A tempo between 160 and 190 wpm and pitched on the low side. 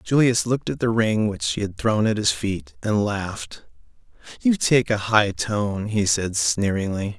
Yes: average, 185 wpm; low, 105 Hz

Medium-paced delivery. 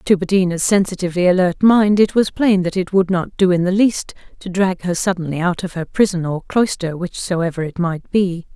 No: fast, 210 wpm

